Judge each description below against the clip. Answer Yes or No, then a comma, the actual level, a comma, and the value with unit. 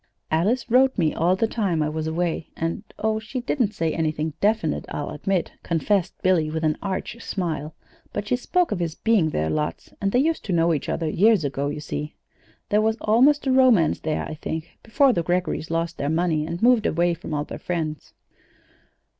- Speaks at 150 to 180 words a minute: No, average, 200 wpm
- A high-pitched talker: No, medium, 175 Hz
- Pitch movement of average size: No, wide, 5.7 semitones